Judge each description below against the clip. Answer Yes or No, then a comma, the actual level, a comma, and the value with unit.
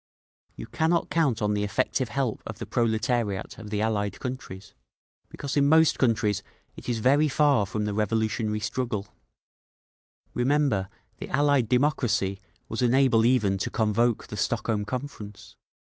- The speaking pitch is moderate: No, low, 115 Hz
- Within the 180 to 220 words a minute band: No, average, 145 wpm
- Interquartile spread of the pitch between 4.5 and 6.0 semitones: No, average, 3.9 semitones